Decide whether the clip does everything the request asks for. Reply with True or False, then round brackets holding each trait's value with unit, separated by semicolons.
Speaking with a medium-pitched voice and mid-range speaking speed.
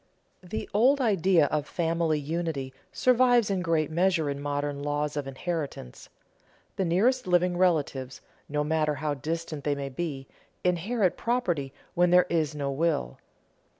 True (160 Hz; 145 wpm)